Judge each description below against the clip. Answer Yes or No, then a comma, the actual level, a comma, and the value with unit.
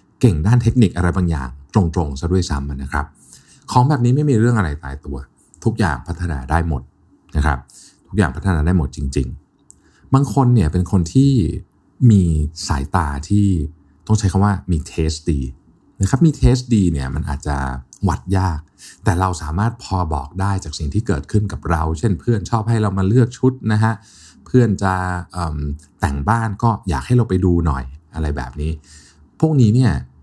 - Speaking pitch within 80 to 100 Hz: Yes, very low, 90 Hz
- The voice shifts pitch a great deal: Yes, wide, 6.1 semitones